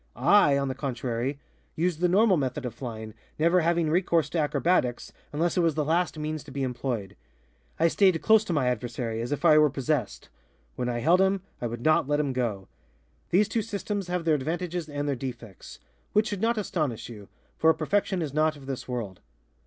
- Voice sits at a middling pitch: Yes, medium, 150 Hz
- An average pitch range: No, wide, 5.8 semitones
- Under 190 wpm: No, average, 200 wpm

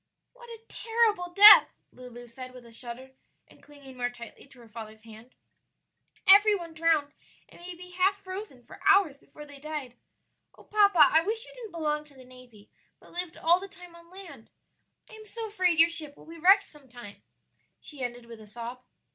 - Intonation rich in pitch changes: Yes, wide, 7.1 semitones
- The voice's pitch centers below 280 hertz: No, very high, 310 Hz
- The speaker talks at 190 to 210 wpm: Yes, average, 195 wpm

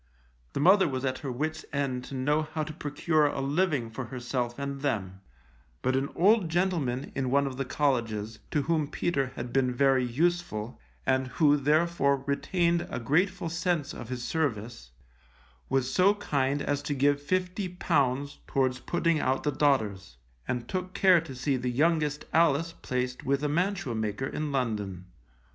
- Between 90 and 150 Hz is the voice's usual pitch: Yes, medium, 140 Hz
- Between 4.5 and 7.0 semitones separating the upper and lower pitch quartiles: No, average, 4.1 semitones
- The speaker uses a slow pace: No, average, 170 wpm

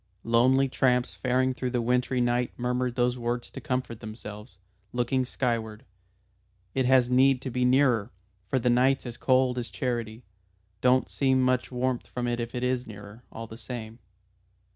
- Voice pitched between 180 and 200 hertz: No, low, 125 Hz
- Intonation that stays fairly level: Yes, narrow, 1.5 semitones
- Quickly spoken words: No, average, 165 wpm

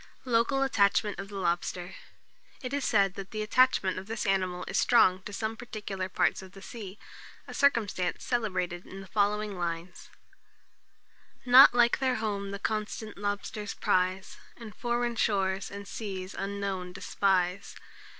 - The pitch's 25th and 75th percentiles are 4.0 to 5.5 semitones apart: No, average, 2.9 semitones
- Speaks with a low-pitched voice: No, high, 200 Hz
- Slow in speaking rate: No, average, 150 wpm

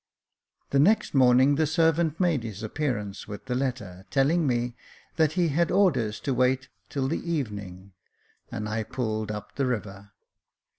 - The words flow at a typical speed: Yes, average, 155 wpm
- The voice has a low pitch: Yes, low, 130 Hz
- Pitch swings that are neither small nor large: No, wide, 6.0 semitones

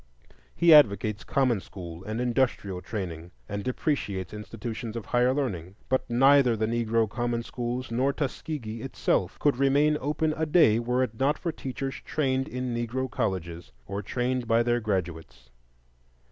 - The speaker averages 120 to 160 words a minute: Yes, average, 150 wpm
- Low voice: Yes, low, 120 Hz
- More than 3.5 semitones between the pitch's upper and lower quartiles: Yes, average, 4.3 semitones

